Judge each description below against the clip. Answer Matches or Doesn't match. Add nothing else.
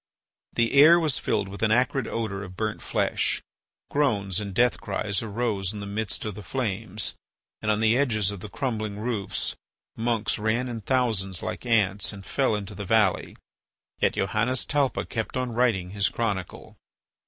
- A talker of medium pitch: Doesn't match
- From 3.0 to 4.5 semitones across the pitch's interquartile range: Matches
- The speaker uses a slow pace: Doesn't match